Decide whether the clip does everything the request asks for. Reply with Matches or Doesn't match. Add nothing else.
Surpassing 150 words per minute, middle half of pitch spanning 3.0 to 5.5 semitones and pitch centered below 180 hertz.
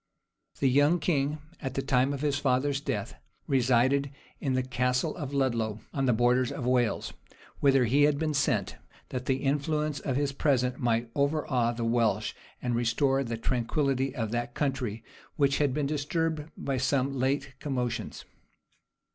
Doesn't match